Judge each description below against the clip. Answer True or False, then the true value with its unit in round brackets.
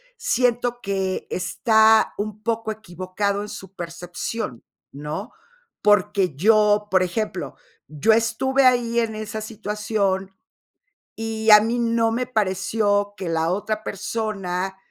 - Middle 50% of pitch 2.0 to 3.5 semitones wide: True (2.9 semitones)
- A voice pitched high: True (210 Hz)